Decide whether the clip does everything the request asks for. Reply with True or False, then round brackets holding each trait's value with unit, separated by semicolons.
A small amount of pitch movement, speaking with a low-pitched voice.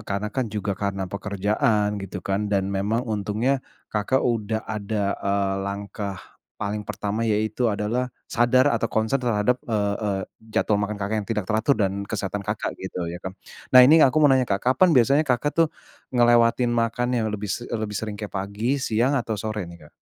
False (3.0 semitones; 105 Hz)